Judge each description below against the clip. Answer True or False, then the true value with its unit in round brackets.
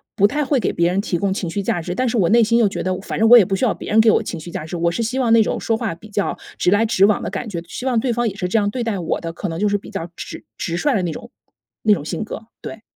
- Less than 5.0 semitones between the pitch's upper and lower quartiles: True (4.2 semitones)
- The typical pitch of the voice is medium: False (205 Hz)